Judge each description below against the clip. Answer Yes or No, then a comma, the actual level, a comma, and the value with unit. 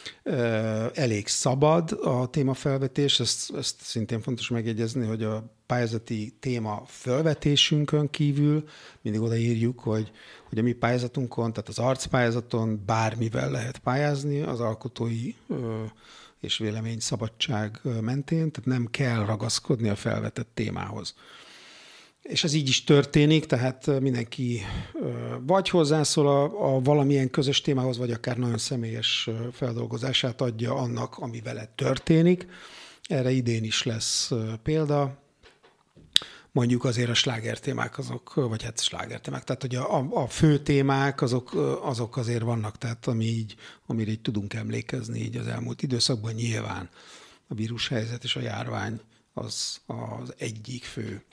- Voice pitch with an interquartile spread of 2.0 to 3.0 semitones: No, average, 3.4 semitones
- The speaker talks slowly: No, average, 130 wpm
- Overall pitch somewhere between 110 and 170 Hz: Yes, low, 120 Hz